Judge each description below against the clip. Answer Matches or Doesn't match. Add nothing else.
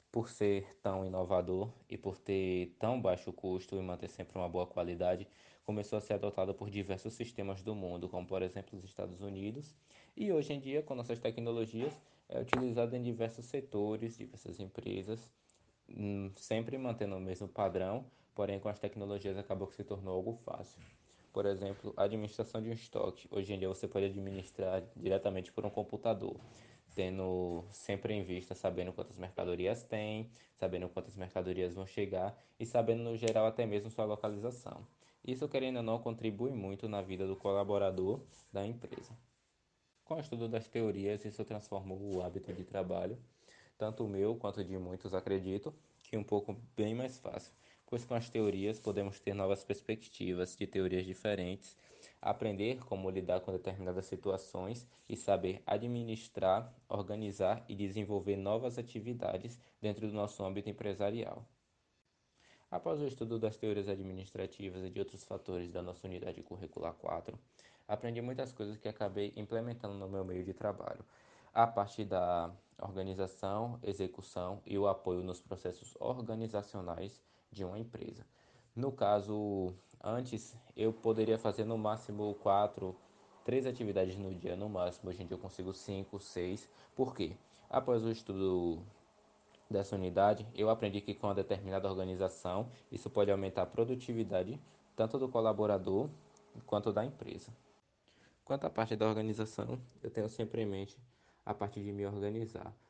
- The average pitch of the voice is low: Matches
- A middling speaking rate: Matches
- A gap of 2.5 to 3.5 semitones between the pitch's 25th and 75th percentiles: Matches